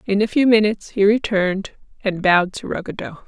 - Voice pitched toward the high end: Yes, high, 200 Hz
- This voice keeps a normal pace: Yes, average, 185 wpm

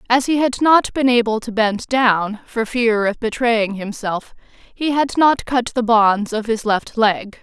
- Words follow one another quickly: No, average, 195 wpm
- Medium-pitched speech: No, high, 230 Hz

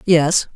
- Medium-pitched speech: Yes, medium, 160 Hz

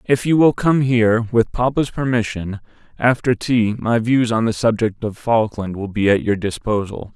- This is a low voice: Yes, low, 115 Hz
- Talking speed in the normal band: Yes, average, 170 wpm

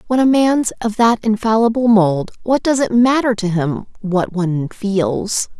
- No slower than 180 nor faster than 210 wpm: No, average, 170 wpm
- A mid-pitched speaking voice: No, high, 215 Hz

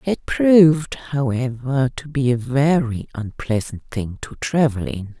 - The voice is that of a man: No, female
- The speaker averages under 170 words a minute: Yes, average, 140 wpm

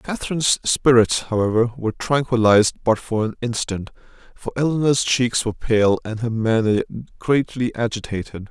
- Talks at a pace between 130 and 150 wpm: Yes, slow, 135 wpm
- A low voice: Yes, low, 115 Hz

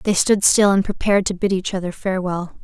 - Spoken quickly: Yes, fast, 225 wpm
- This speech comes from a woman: Yes, female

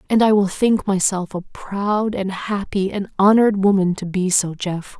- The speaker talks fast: No, average, 190 wpm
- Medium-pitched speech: No, high, 195 Hz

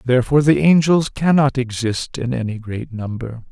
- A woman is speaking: No, male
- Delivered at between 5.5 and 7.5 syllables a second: No, 5.0 syllables/s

